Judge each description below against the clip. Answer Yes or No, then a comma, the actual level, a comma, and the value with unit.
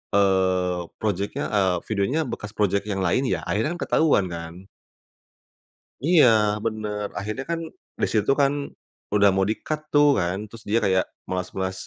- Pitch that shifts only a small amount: No, average, 3.2 semitones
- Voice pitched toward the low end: Yes, low, 100 Hz